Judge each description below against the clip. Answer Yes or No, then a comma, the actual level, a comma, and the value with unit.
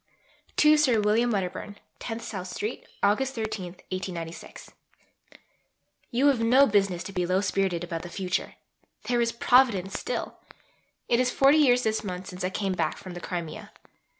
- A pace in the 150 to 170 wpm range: Yes, average, 155 wpm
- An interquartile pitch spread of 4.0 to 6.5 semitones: Yes, average, 4.9 semitones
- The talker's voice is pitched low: No, high, 205 Hz